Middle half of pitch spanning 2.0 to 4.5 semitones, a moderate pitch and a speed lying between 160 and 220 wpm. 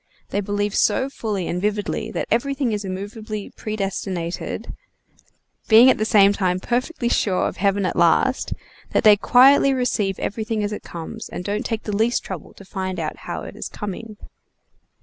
No: average, 2.8 semitones; high, 210 Hz; average, 170 wpm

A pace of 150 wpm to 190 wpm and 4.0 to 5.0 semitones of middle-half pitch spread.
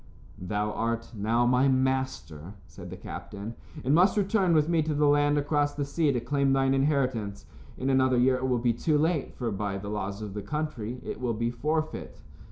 No: average, 200 wpm; average, 4.5 semitones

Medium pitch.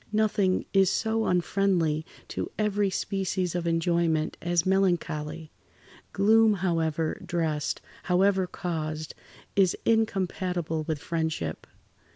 Yes: medium, 180 Hz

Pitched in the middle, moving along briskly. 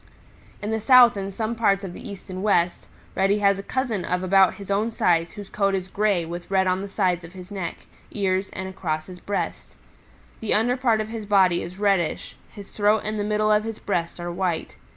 No: high, 195 Hz; fast, 220 wpm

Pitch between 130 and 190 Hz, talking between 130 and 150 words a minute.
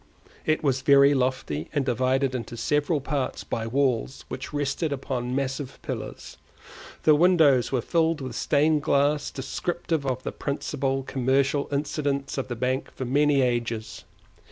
Yes: low, 135 Hz; average, 145 wpm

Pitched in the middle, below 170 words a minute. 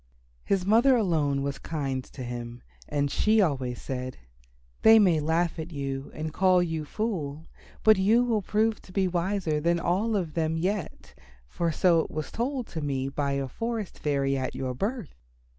No: medium, 165 Hz; average, 175 wpm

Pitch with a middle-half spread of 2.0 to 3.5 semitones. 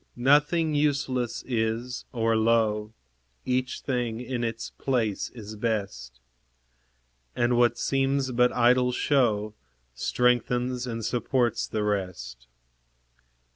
Yes: narrow, 2.4 semitones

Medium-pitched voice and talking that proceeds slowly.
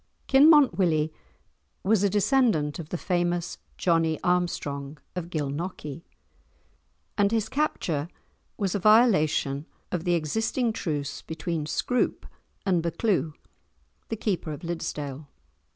Yes: medium, 175 Hz; slow, 115 wpm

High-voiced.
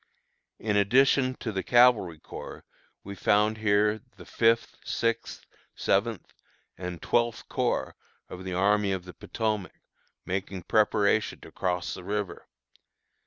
No: low, 105 Hz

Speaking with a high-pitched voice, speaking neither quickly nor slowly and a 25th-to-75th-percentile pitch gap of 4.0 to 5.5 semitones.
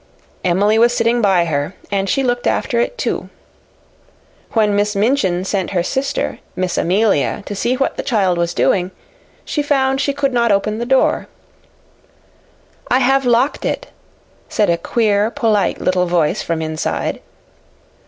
Yes: high, 210 Hz; average, 155 wpm; average, 5.2 semitones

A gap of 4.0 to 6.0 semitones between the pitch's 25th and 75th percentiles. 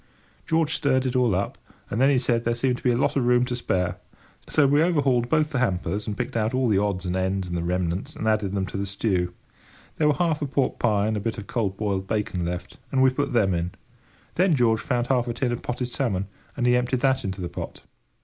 Yes: average, 5.1 semitones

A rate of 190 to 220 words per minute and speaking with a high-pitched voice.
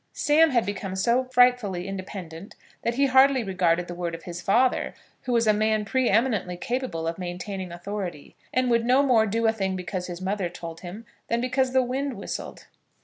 Yes: average, 195 wpm; high, 210 Hz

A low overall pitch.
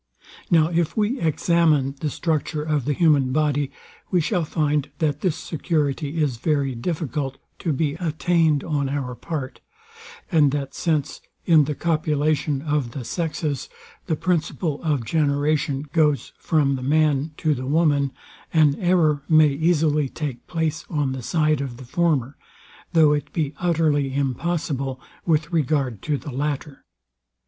No: medium, 150 Hz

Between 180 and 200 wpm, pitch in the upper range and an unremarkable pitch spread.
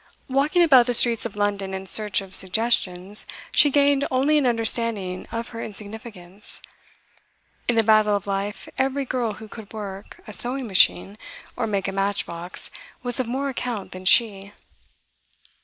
No: average, 155 wpm; high, 215 Hz; average, 3.8 semitones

